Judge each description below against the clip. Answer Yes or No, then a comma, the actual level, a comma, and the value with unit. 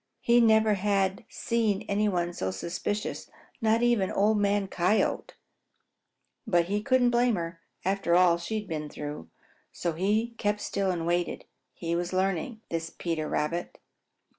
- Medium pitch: No, high, 195 Hz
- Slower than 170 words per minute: Yes, average, 150 wpm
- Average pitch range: Yes, average, 3.9 semitones